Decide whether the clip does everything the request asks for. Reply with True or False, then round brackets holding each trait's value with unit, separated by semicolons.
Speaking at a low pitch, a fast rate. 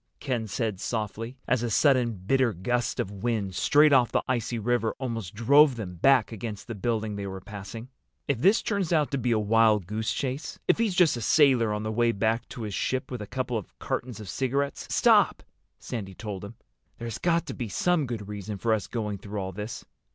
True (115 Hz; 210 wpm)